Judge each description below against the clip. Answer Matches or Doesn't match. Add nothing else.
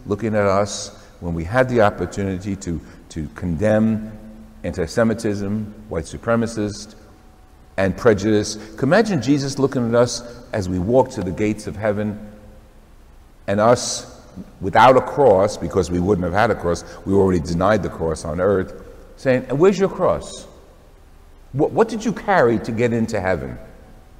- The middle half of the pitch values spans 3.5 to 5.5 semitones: Matches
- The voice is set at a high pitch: Doesn't match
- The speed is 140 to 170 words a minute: Matches